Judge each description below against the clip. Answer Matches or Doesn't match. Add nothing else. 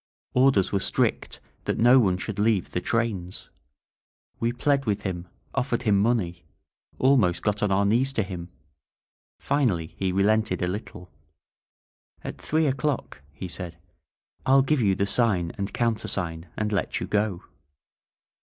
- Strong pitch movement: Doesn't match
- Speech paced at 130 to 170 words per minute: Matches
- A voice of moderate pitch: Doesn't match